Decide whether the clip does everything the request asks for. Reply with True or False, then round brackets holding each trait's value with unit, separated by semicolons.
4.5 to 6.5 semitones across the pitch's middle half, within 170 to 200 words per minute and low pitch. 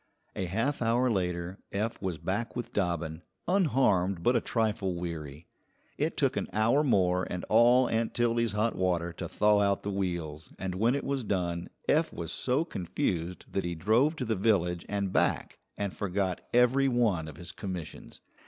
True (5.0 semitones; 175 wpm; 100 Hz)